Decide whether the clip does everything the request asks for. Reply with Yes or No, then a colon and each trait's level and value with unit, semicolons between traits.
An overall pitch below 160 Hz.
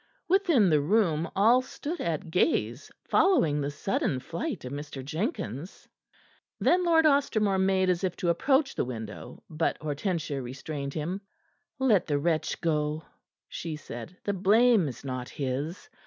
No: medium, 170 Hz